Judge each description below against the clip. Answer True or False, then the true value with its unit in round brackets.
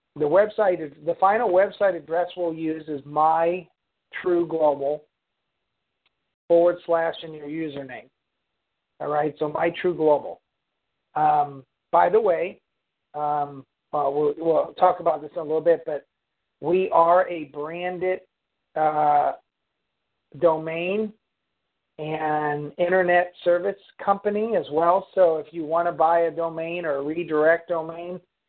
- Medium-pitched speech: True (165 Hz)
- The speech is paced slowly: True (125 wpm)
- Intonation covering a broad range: False (2.6 semitones)